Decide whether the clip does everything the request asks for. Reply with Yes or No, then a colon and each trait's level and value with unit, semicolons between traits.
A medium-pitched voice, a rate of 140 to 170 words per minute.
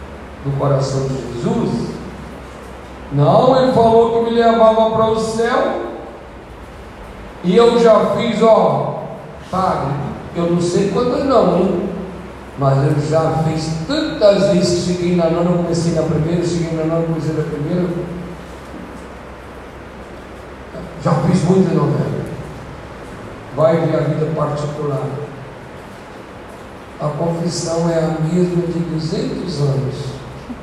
No: medium, 165 Hz; slow, 120 wpm